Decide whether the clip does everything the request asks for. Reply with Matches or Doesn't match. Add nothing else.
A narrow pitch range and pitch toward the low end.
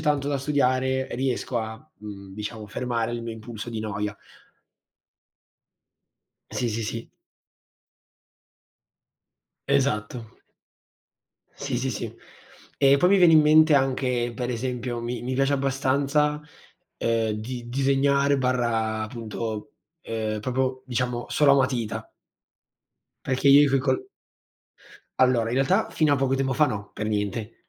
Doesn't match